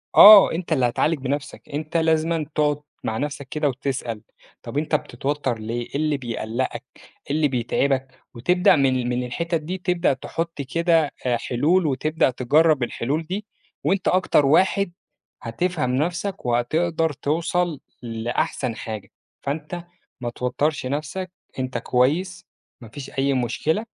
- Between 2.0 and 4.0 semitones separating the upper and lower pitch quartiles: No, average, 4.7 semitones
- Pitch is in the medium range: Yes, medium, 145 Hz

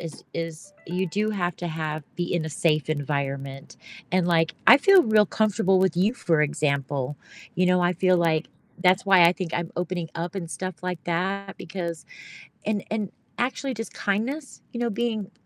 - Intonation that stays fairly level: No, average, 3.4 semitones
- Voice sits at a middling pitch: Yes, medium, 180 Hz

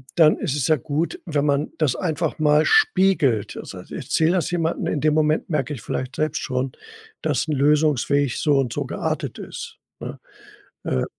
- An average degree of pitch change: No, narrow, 2.2 semitones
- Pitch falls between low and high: Yes, medium, 150 Hz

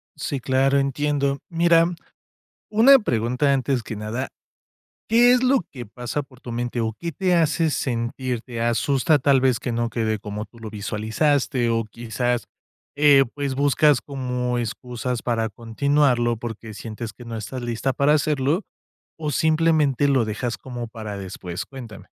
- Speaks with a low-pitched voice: Yes, low, 125 Hz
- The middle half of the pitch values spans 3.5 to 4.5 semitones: Yes, average, 3.8 semitones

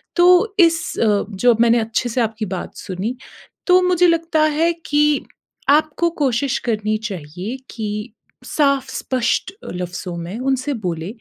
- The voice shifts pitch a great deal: Yes, wide, 6.7 semitones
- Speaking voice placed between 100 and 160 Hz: No, high, 245 Hz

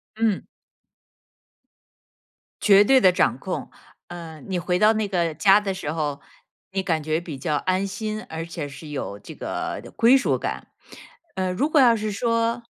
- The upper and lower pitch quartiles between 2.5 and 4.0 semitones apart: No, average, 5.0 semitones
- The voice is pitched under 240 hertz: Yes, medium, 185 Hz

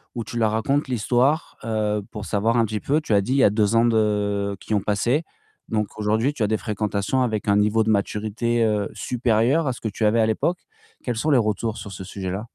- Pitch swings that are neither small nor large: No, narrow, 2.3 semitones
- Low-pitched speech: Yes, low, 110 Hz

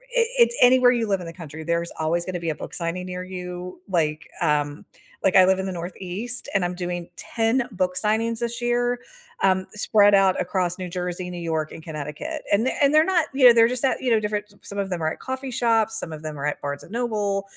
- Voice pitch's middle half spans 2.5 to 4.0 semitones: No, average, 5.2 semitones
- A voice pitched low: No, high, 190 Hz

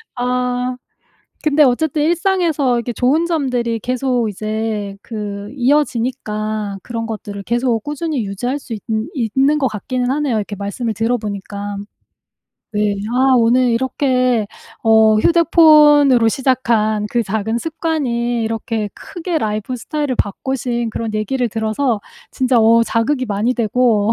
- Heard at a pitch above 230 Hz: Yes, high, 240 Hz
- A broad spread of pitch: No, average, 3.5 semitones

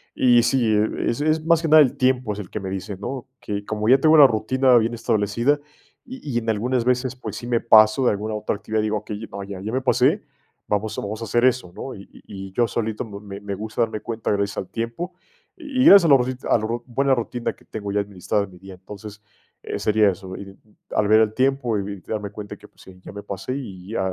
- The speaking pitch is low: Yes, low, 110 Hz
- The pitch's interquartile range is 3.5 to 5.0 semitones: Yes, average, 3.8 semitones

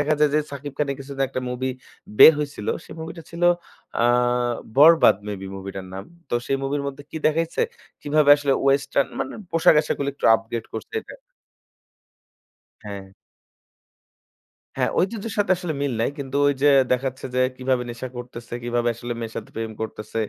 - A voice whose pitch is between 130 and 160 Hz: Yes, low, 135 Hz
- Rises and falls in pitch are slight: No, average, 3.9 semitones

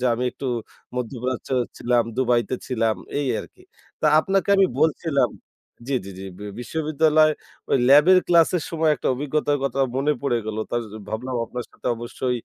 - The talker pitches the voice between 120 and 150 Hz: Yes, low, 135 Hz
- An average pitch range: Yes, average, 4.1 semitones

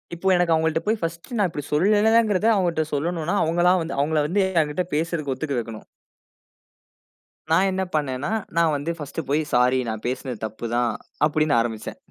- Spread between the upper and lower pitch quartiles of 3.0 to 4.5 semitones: Yes, average, 4.1 semitones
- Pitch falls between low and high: Yes, medium, 160 Hz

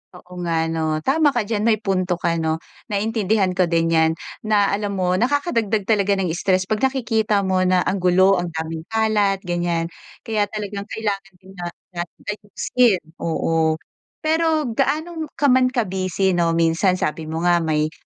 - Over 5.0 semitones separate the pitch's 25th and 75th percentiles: No, average, 4.0 semitones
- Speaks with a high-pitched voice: Yes, high, 195 Hz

